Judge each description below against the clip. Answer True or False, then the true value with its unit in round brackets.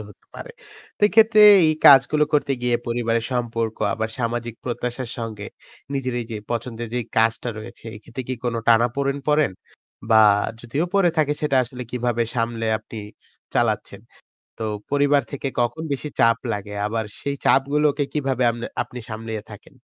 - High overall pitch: False (120 Hz)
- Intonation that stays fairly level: False (3.4 semitones)